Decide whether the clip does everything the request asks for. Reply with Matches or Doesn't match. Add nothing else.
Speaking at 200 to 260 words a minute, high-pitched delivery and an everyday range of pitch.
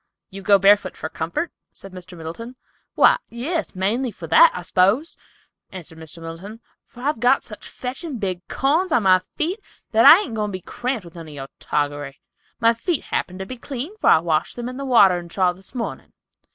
Doesn't match